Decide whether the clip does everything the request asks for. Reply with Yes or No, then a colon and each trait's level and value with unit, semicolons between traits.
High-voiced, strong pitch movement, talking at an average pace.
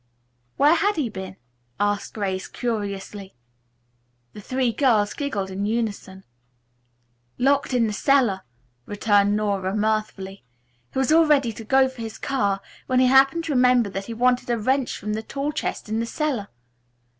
No: high, 225 Hz; average, 4.5 semitones; average, 160 wpm